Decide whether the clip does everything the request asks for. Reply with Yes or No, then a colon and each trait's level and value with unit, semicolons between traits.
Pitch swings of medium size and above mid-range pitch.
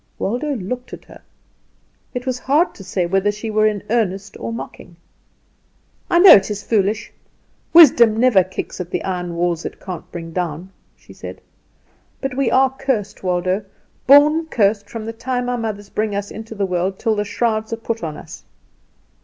Yes: average, 4.4 semitones; high, 215 Hz